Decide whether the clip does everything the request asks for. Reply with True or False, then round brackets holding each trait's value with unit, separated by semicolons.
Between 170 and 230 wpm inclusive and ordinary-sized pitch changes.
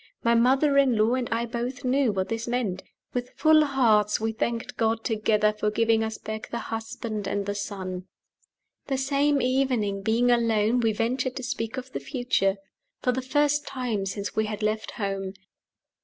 True (180 wpm; 3.2 semitones)